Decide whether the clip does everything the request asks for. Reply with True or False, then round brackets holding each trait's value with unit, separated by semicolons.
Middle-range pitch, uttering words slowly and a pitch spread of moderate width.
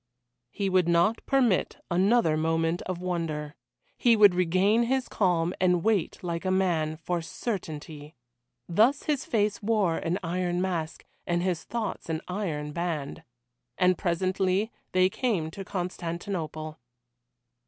True (180 Hz; 130 wpm; 3.4 semitones)